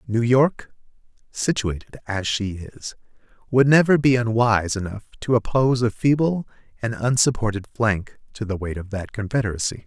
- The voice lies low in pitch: Yes, low, 115 Hz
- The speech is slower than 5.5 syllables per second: Yes, 5.1 syllables/s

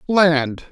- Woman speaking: No, male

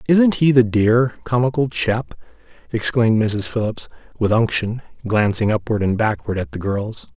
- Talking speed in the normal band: Yes, average, 150 wpm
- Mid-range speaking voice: No, low, 110 Hz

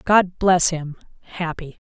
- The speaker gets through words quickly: No, slow, 95 wpm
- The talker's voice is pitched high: No, medium, 170 Hz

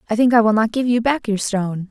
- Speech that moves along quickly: Yes, fast, 315 wpm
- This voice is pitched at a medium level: No, high, 225 Hz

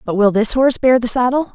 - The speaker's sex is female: Yes, female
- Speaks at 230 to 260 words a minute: No, fast, 270 wpm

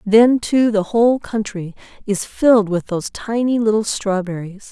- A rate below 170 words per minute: Yes, average, 155 wpm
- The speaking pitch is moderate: No, high, 215 Hz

